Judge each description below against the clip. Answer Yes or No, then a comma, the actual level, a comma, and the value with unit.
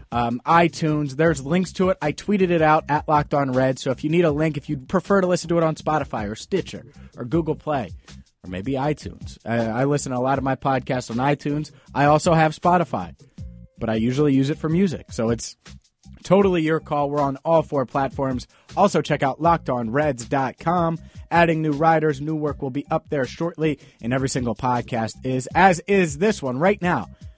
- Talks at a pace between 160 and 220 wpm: Yes, fast, 205 wpm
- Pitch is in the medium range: Yes, medium, 145 Hz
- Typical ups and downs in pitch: Yes, average, 4.1 semitones